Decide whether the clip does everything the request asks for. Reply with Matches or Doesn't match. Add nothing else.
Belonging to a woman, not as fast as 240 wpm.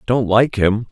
Doesn't match